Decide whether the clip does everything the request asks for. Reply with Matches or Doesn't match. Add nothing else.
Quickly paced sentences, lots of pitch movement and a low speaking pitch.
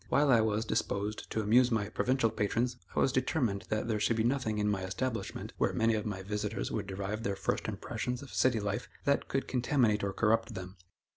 Doesn't match